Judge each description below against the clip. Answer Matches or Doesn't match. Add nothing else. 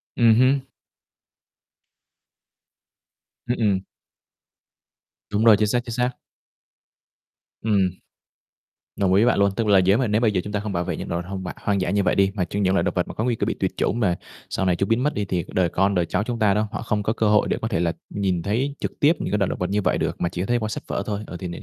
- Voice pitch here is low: Matches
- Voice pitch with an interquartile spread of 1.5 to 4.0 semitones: Matches